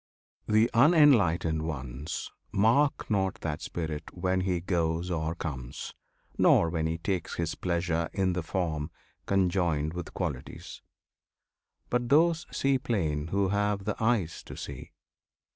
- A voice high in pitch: No, very low, 90 Hz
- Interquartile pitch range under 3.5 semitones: No, average, 4.3 semitones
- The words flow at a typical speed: No, slow, 130 wpm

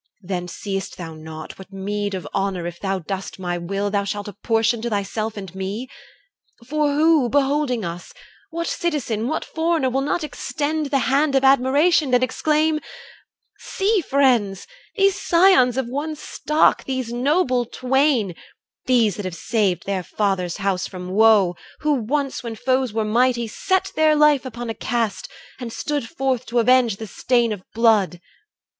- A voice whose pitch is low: No, high, 235 Hz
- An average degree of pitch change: No, wide, 6.1 semitones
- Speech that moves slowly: No, average, 160 wpm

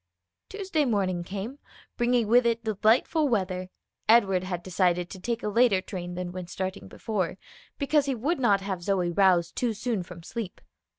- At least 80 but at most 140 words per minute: No, average, 170 wpm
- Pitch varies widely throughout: No, average, 4.5 semitones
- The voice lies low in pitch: No, high, 200 Hz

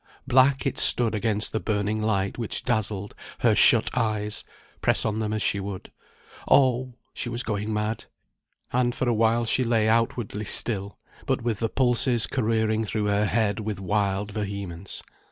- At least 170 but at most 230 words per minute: No, average, 160 wpm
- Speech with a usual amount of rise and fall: No, narrow, 2.3 semitones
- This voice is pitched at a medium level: No, low, 110 Hz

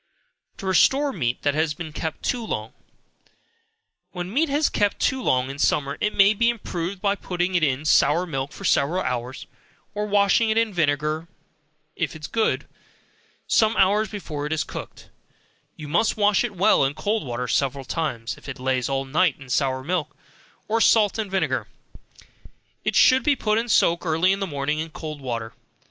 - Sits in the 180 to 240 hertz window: No, medium, 170 Hz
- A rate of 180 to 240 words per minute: Yes, average, 185 wpm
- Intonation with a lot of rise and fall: Yes, wide, 6.8 semitones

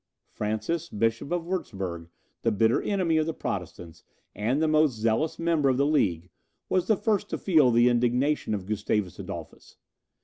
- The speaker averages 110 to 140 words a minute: No, average, 165 wpm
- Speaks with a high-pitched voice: No, low, 125 Hz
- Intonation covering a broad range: Yes, wide, 7.2 semitones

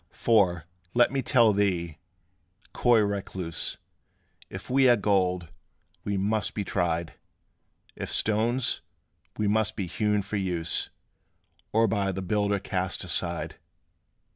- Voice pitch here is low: Yes, low, 100 Hz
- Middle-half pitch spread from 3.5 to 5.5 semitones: No, average, 3.1 semitones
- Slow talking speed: Yes, slow, 120 wpm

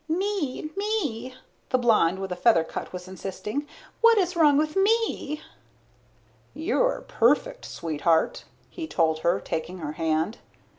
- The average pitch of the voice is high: Yes, very high, 255 Hz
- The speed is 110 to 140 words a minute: Yes, slow, 135 wpm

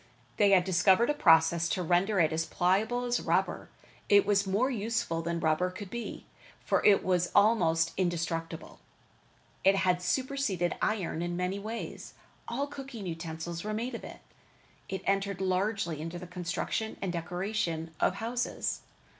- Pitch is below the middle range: No, medium, 185 Hz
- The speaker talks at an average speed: Yes, average, 155 wpm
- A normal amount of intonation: Yes, average, 3.9 semitones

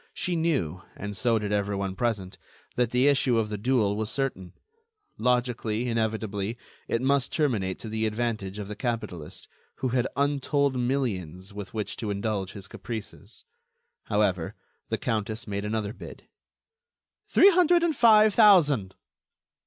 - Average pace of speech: Yes, average, 145 wpm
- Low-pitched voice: Yes, low, 110 Hz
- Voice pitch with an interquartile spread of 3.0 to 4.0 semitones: No, average, 4.4 semitones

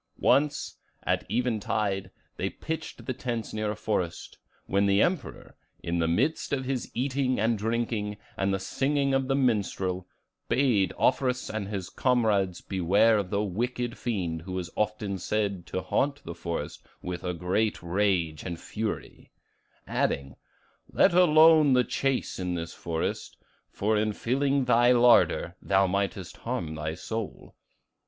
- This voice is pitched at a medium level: No, low, 105 Hz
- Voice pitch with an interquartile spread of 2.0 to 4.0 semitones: No, average, 5.3 semitones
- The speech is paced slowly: No, average, 145 wpm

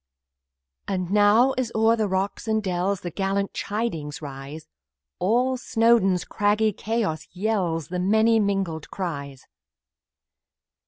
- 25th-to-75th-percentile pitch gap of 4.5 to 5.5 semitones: No, average, 3.9 semitones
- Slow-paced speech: Yes, slow, 110 wpm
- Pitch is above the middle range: Yes, high, 200 Hz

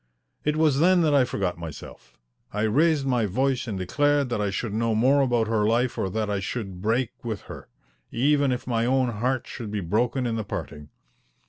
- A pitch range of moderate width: Yes, average, 4.2 semitones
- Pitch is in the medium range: No, low, 120 Hz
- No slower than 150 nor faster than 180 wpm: No, fast, 205 wpm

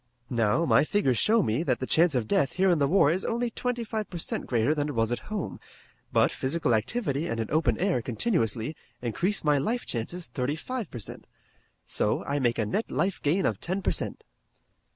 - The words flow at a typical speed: No, fast, 215 wpm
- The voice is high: No, medium, 150 Hz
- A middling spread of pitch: No, wide, 8.0 semitones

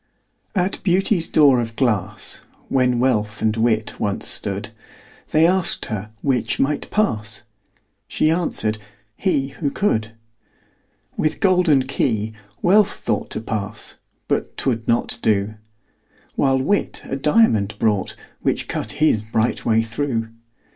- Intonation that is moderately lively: No, wide, 6.0 semitones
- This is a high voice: No, low, 120 Hz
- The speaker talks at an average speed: No, slow, 125 wpm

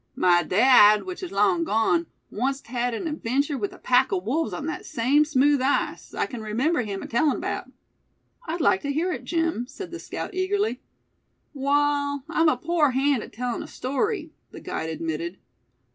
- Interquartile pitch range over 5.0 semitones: Yes, wide, 5.6 semitones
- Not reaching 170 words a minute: No, average, 180 wpm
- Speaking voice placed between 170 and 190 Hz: No, very high, 275 Hz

